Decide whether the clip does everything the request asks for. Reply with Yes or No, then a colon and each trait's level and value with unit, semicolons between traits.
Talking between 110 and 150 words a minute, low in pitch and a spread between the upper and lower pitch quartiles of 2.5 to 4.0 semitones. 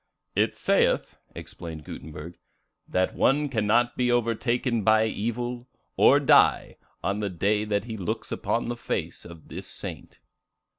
Yes: average, 140 wpm; low, 110 Hz; average, 3.6 semitones